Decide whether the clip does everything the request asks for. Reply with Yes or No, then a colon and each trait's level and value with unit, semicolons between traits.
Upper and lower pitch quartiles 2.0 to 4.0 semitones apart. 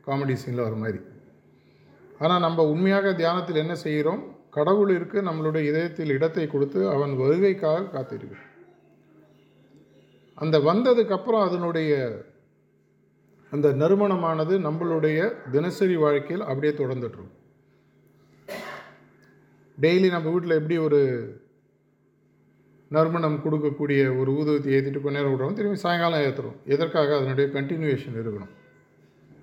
Yes: average, 3.6 semitones